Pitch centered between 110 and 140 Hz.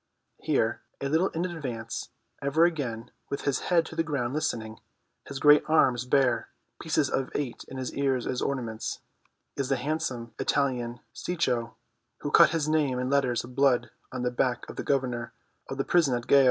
Yes: low, 135 Hz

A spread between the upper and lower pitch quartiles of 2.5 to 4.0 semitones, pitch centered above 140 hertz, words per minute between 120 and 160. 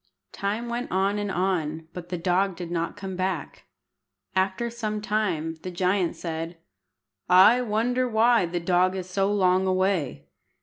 Yes: average, 2.8 semitones; high, 190 Hz; average, 150 wpm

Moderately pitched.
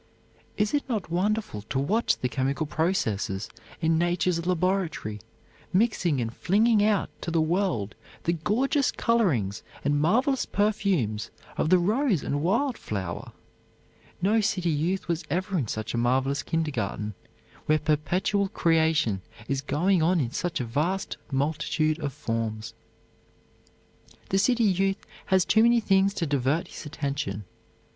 Yes: medium, 165 Hz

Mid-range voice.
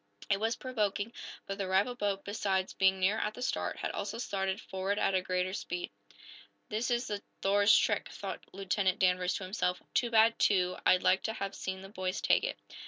No: high, 195 Hz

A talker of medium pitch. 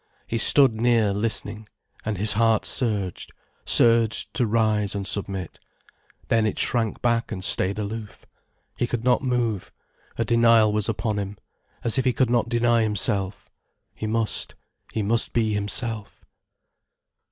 No: low, 110 Hz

